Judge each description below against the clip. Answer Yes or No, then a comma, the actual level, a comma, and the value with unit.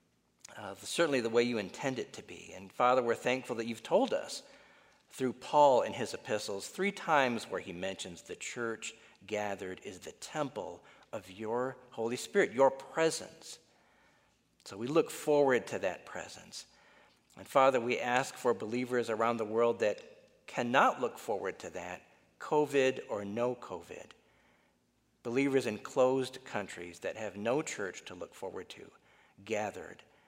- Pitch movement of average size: Yes, average, 4.5 semitones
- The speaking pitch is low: Yes, low, 125 Hz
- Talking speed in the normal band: Yes, average, 155 wpm